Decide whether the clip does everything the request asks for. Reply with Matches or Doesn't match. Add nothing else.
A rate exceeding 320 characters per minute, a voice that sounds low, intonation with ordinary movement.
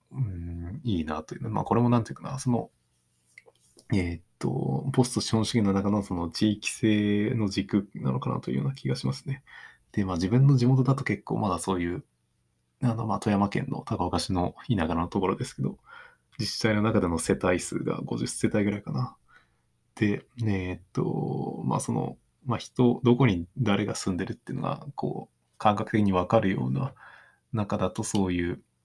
Matches